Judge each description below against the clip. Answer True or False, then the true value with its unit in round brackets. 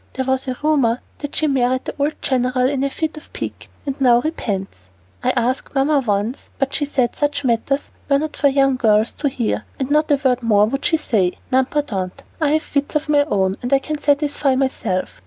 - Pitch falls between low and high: False (270 Hz)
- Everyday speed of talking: False (210 wpm)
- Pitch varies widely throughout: False (3.1 semitones)